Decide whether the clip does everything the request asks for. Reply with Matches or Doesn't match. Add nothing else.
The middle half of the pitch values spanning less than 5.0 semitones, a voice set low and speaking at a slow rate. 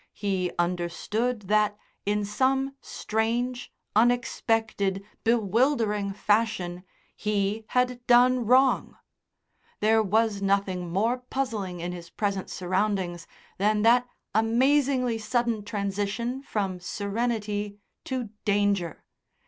Doesn't match